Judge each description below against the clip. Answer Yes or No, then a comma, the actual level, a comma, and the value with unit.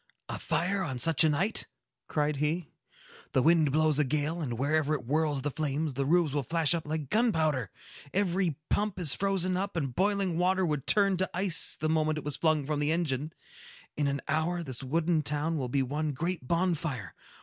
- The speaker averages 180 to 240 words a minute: Yes, average, 195 wpm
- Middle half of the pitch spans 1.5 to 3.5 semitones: Yes, average, 3.2 semitones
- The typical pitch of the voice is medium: Yes, medium, 155 Hz